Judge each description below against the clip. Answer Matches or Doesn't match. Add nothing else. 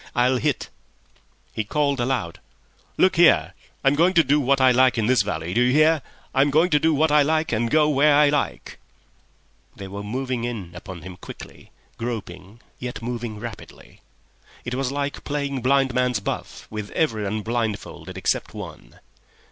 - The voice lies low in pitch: Matches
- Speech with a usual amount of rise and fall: Matches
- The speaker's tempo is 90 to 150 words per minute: Doesn't match